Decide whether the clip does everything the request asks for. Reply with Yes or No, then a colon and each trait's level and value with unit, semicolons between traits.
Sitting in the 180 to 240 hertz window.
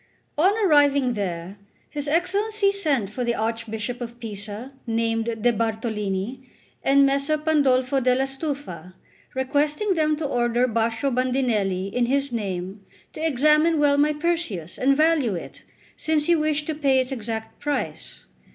No: very high, 260 Hz